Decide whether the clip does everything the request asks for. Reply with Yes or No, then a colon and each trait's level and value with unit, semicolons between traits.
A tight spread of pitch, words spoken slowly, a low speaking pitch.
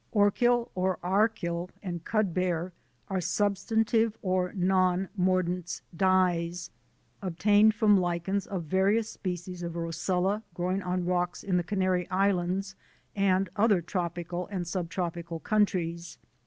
No: narrow, 2.2 semitones; slow, 120 wpm; medium, 185 Hz